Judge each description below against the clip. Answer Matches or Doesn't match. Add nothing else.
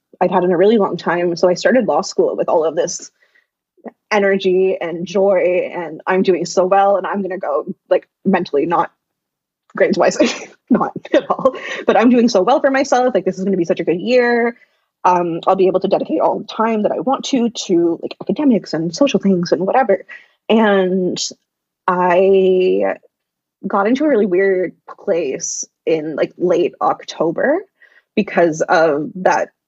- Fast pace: Doesn't match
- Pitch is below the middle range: Doesn't match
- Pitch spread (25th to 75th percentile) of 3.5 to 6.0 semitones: Matches